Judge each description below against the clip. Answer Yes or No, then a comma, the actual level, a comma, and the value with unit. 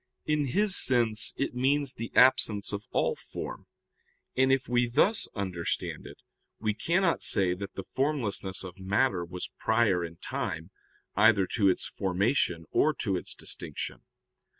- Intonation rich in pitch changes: Yes, wide, 5.8 semitones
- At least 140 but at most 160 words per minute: Yes, average, 150 wpm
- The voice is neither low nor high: No, low, 110 Hz